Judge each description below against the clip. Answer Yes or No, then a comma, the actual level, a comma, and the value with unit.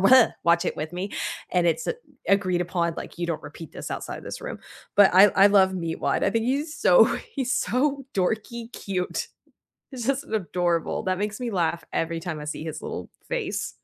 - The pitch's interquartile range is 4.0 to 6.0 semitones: Yes, wide, 5.5 semitones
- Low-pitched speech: No, high, 190 Hz